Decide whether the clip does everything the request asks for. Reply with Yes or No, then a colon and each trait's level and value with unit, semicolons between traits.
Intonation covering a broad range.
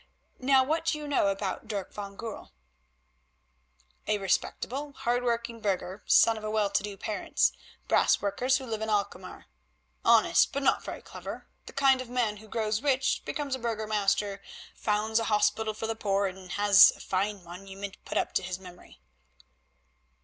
No: average, 3.3 semitones